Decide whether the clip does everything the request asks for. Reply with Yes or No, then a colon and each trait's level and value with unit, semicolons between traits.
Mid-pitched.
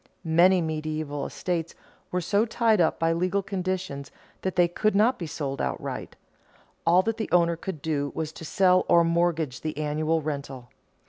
Yes: medium, 170 Hz